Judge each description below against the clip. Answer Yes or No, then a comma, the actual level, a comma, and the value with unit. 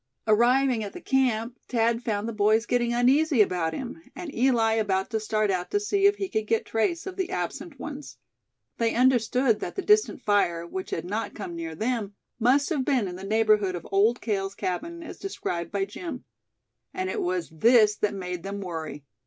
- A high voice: Yes, high, 225 Hz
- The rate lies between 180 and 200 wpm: Yes, average, 195 wpm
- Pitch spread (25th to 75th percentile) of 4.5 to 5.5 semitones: Yes, average, 5.2 semitones